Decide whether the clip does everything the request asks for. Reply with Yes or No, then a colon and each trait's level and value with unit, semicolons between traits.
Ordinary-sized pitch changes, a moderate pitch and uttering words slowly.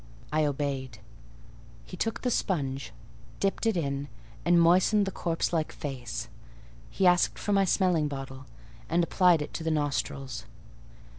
No: average, 4.7 semitones; medium, 155 Hz; average, 145 wpm